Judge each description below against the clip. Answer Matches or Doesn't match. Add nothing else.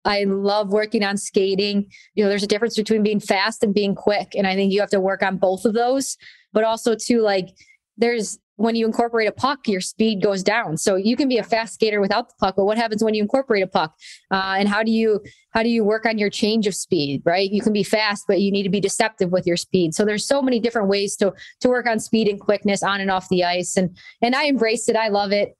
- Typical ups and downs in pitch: Doesn't match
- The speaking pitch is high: Matches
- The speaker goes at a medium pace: Doesn't match